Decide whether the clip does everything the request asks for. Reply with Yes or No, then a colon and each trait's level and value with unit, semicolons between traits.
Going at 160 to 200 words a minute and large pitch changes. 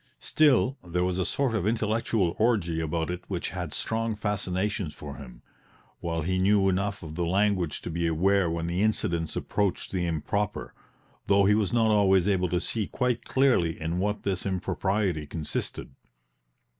No: average, 170 wpm; average, 3.6 semitones